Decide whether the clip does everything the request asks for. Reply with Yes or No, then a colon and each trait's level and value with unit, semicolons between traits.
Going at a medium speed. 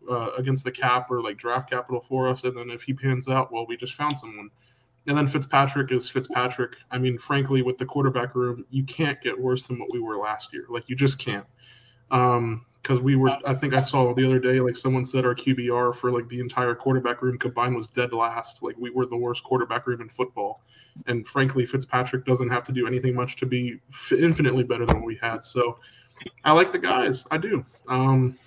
No: fast, 225 wpm